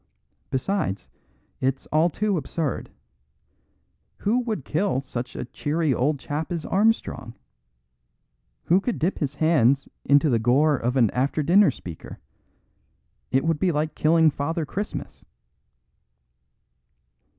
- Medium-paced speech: No, slow, 120 wpm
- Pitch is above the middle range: No, medium, 150 Hz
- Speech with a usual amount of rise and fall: Yes, average, 4.4 semitones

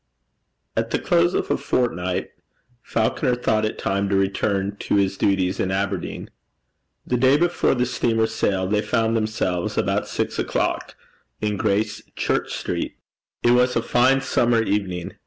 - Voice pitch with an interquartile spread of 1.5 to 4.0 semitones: Yes, average, 3.6 semitones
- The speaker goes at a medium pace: Yes, average, 150 wpm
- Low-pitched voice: Yes, low, 105 Hz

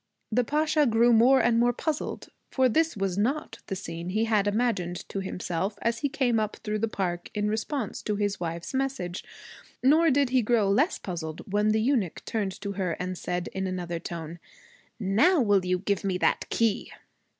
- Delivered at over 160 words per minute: Yes, average, 190 wpm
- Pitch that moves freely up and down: No, average, 4.8 semitones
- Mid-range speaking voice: No, high, 210 Hz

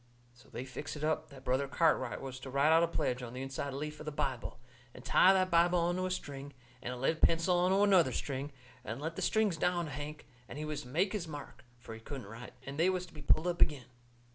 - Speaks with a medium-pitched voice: Yes, medium, 150 Hz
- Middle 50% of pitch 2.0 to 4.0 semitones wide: No, average, 4.4 semitones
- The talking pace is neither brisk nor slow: No, fast, 255 wpm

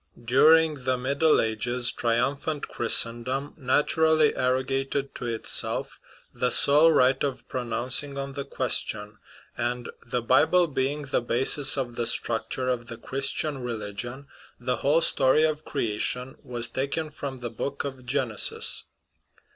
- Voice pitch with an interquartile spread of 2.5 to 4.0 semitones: Yes, average, 2.8 semitones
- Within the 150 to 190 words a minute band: No, average, 140 wpm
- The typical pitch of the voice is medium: No, low, 130 Hz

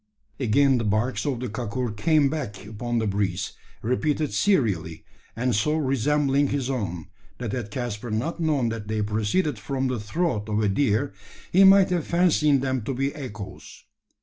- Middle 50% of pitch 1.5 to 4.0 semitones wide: No, average, 5.3 semitones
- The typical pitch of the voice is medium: No, low, 125 Hz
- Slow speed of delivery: No, average, 170 wpm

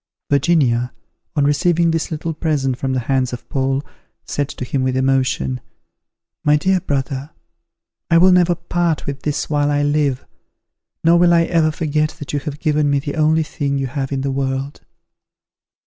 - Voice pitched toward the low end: No, medium, 145 Hz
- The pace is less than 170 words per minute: No, average, 175 wpm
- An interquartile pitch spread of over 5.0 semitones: No, average, 3.0 semitones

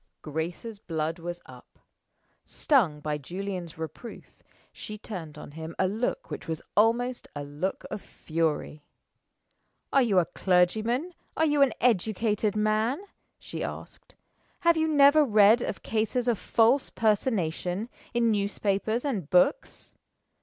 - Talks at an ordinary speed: No, slow, 130 wpm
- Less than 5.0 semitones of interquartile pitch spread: No, wide, 5.6 semitones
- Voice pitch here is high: Yes, high, 210 Hz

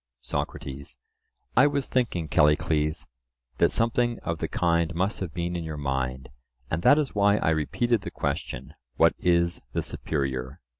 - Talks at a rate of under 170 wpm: Yes, average, 150 wpm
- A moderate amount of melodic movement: No, wide, 5.7 semitones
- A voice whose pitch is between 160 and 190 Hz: No, very low, 85 Hz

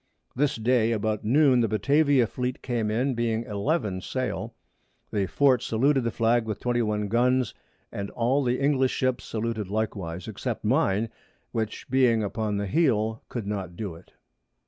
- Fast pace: No, average, 155 wpm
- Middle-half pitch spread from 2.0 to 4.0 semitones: Yes, average, 3.3 semitones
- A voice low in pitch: Yes, low, 115 Hz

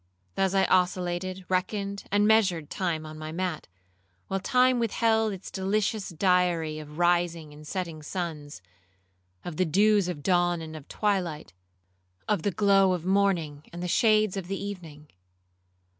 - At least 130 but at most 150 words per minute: Yes, average, 145 wpm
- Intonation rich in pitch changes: No, average, 4.1 semitones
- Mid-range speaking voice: Yes, medium, 180 Hz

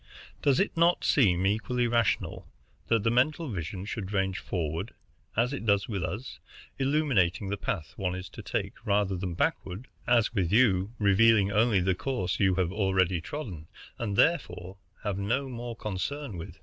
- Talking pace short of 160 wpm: No, average, 165 wpm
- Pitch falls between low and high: No, low, 100 Hz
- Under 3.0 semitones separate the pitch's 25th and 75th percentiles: No, average, 4.3 semitones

